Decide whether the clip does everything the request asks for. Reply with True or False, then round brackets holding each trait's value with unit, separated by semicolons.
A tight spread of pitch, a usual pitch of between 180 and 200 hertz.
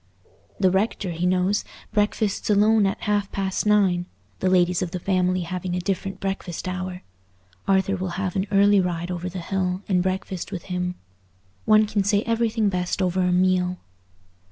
True (1.9 semitones; 185 Hz)